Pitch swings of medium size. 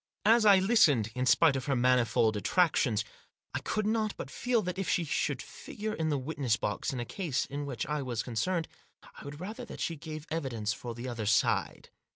No: wide, 7.0 semitones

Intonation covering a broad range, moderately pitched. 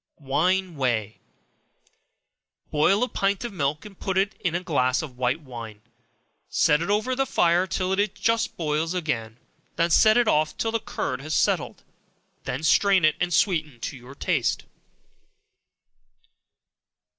Yes: wide, 5.9 semitones; medium, 165 Hz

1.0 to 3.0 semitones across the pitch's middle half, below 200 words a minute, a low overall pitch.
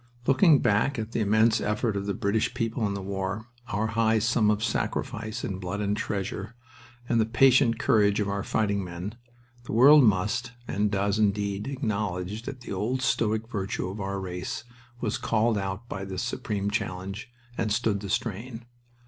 Yes: narrow, 2.5 semitones; average, 175 wpm; low, 105 Hz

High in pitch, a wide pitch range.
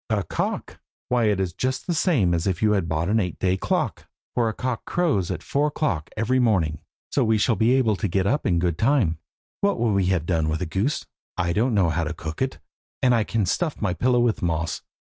No: low, 105 Hz; wide, 6.1 semitones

